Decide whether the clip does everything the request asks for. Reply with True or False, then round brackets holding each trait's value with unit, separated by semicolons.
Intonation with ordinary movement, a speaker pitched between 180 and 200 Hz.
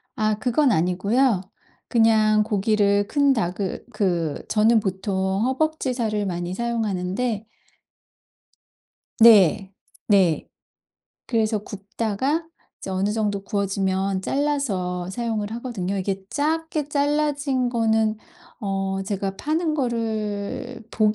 False (4.0 semitones; 215 Hz)